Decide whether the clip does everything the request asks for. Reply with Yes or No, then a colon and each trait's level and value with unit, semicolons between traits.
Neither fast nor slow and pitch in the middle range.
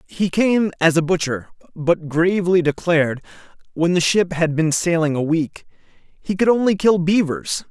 Yes: average, 165 wpm; medium, 170 Hz